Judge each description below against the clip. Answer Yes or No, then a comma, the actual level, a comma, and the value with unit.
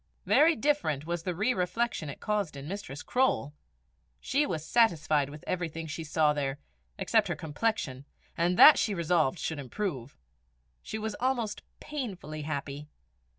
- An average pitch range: No, wide, 6.6 semitones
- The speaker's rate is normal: Yes, average, 150 wpm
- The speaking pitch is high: No, medium, 170 Hz